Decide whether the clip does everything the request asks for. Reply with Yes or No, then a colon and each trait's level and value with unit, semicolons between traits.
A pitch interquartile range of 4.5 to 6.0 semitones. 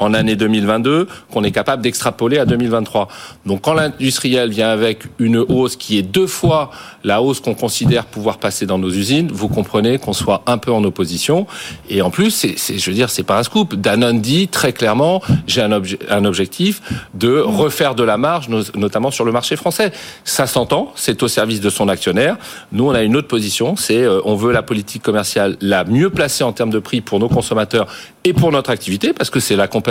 No: average, 4.0 semitones